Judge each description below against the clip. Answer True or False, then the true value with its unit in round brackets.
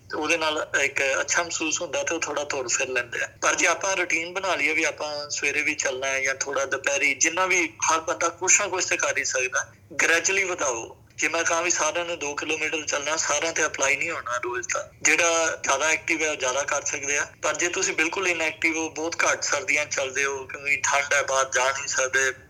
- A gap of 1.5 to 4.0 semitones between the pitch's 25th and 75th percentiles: True (2.9 semitones)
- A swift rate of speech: True (215 wpm)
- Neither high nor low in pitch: True (160 Hz)